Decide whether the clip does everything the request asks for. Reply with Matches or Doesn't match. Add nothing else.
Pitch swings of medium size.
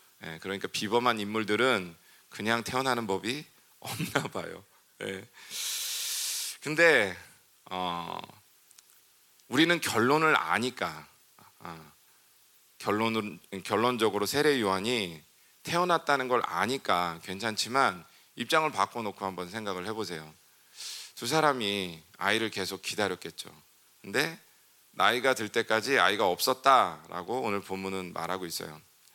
Matches